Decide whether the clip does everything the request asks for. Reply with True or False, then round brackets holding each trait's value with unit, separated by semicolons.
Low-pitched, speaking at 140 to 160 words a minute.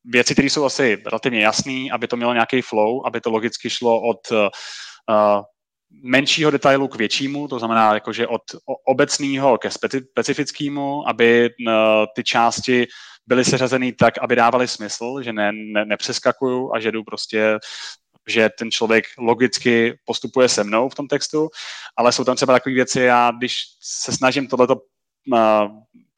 True (120 Hz; 155 wpm)